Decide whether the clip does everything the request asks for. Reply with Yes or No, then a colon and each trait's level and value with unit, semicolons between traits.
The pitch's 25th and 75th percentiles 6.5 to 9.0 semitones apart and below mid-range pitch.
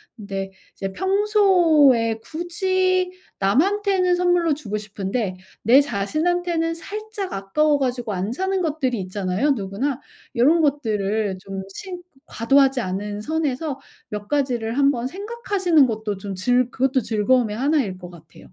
No: wide, 8.6 semitones; very high, 265 Hz